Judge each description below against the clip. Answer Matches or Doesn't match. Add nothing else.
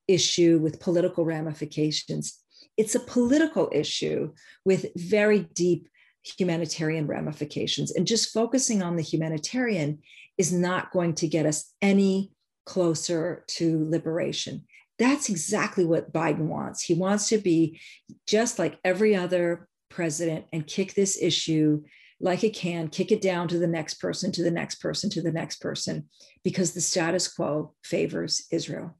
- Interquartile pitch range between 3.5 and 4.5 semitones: Doesn't match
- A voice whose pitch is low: Doesn't match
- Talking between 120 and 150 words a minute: Matches